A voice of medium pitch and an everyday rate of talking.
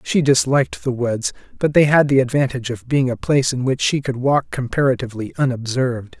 No: low, 125 Hz; average, 195 wpm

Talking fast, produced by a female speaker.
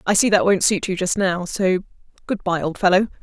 Yes: fast, 240 wpm; female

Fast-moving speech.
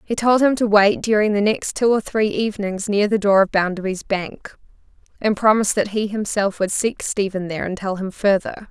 Yes: fast, 215 wpm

